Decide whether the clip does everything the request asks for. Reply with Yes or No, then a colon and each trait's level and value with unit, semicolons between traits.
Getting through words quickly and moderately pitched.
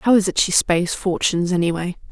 Yes: fast, 225 wpm; medium, 180 Hz